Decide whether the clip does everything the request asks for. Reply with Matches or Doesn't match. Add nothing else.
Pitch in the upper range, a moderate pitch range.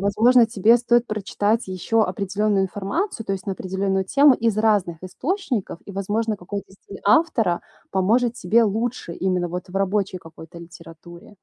Matches